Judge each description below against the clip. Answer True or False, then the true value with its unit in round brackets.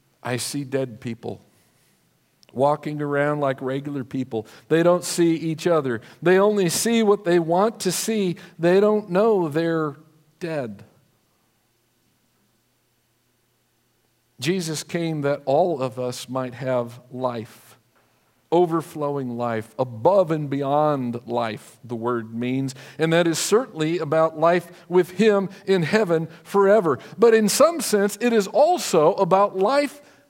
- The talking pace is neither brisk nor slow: False (130 wpm)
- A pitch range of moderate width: False (6.5 semitones)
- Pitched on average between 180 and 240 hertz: False (155 Hz)